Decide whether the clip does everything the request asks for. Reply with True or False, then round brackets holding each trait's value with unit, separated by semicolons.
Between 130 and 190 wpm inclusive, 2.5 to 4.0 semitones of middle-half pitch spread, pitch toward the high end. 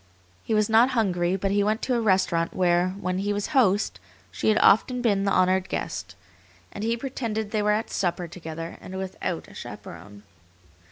True (185 wpm; 3.5 semitones; 195 Hz)